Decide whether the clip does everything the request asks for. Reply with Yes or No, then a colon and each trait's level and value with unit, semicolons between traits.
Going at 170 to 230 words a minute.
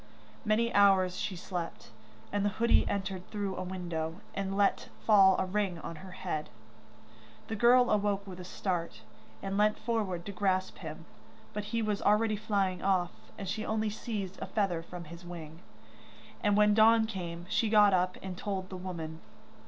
Yes: average, 175 wpm